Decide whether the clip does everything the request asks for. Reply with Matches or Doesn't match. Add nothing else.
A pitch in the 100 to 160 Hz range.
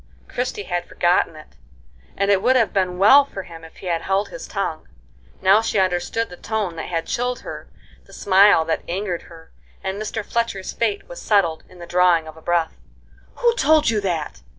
Doesn't match